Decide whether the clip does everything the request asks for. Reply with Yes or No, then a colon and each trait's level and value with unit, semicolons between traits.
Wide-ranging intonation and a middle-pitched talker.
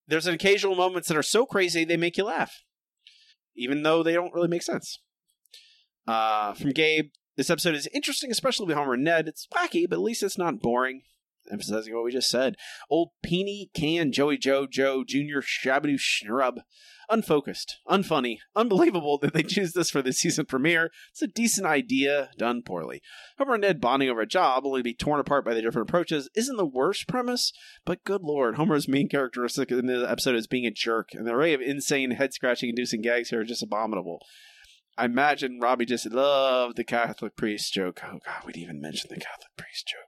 Yes: wide, 6.1 semitones; medium, 145 Hz